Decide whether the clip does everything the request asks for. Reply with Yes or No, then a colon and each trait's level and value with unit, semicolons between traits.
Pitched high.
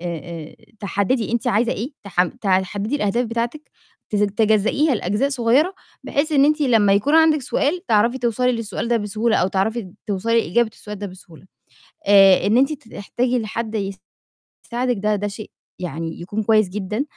Yes: high, 220 Hz